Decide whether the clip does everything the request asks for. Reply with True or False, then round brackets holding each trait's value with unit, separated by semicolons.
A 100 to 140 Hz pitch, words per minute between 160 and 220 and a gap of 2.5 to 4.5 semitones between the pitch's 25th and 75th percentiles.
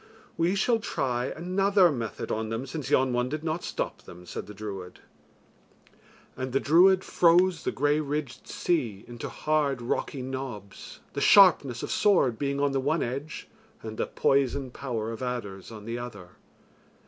False (135 Hz; 165 wpm; 4.9 semitones)